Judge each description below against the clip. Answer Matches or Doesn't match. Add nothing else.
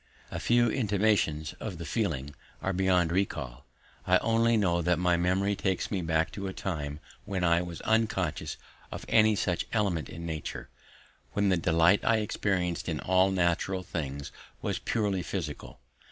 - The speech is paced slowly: Doesn't match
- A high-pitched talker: Doesn't match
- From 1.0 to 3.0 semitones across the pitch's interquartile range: Doesn't match